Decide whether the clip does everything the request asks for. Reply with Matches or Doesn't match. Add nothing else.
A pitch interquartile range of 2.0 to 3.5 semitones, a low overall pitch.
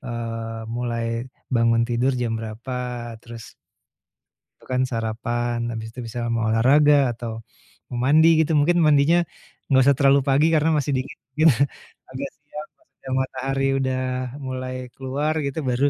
Matches